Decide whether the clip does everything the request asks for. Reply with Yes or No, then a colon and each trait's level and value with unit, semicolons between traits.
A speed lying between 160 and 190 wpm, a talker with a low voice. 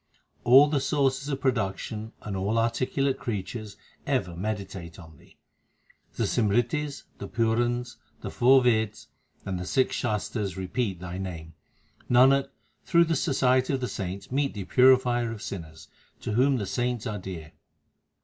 No: average, 150 wpm; low, 115 Hz